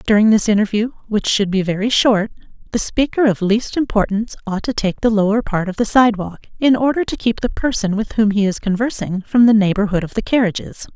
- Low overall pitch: No, high, 215 Hz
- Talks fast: Yes, fast, 220 wpm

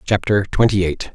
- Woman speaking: No, male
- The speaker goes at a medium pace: Yes, average, 155 wpm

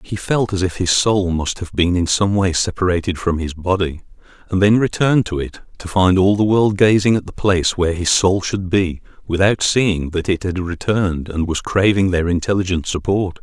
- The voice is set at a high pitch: No, very low, 95 Hz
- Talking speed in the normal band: No, fast, 210 wpm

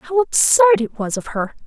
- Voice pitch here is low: No, very high, 265 Hz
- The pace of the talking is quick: Yes, fast, 215 wpm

